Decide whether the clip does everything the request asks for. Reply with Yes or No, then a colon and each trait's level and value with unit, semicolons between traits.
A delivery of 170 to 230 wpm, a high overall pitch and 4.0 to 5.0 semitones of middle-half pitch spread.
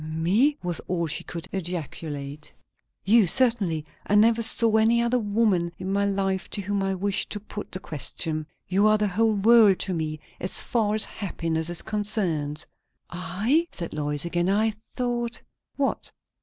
Yes: average, 175 wpm; high, 195 Hz; average, 4.4 semitones